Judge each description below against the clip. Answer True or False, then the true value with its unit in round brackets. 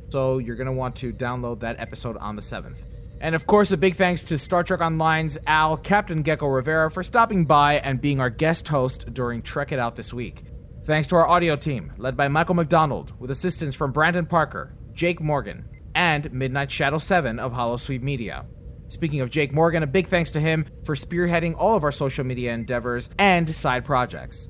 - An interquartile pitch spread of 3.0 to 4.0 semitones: False (4.7 semitones)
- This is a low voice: False (145 Hz)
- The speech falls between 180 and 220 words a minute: True (205 wpm)